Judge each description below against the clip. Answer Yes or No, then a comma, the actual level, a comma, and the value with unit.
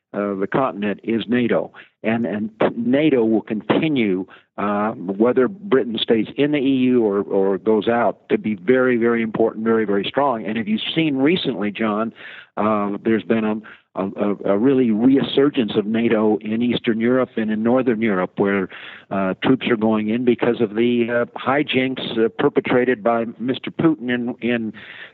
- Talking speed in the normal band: Yes, average, 165 wpm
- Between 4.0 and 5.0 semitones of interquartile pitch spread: No, average, 3.0 semitones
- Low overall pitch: Yes, low, 115 Hz